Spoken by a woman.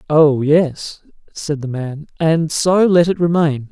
No: male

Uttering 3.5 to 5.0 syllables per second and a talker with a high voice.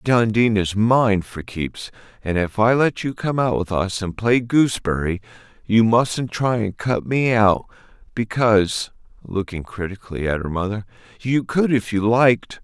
No: 4.5 syllables/s; low, 110 Hz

